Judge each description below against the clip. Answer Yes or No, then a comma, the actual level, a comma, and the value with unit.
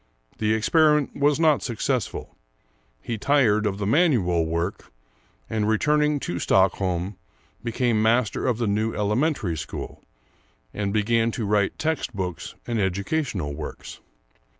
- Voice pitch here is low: Yes, low, 110 Hz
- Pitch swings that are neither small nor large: Yes, average, 5.0 semitones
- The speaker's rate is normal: No, slow, 125 wpm